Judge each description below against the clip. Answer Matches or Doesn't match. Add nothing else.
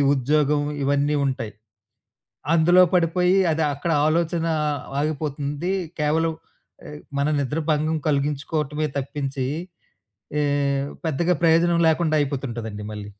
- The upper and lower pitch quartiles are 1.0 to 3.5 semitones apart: Matches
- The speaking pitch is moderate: Matches